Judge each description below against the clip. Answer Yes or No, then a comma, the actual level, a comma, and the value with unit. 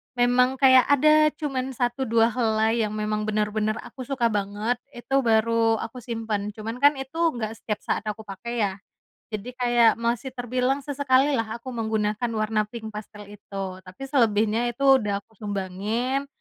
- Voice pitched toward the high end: Yes, high, 230 Hz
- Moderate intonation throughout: Yes, average, 3.2 semitones